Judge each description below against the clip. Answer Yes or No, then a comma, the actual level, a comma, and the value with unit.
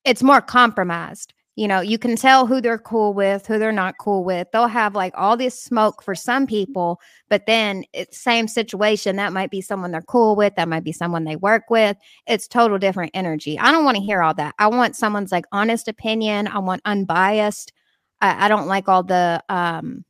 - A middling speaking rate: No, fast, 215 wpm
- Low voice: No, high, 205 Hz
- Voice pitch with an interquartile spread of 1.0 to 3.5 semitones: Yes, average, 3.2 semitones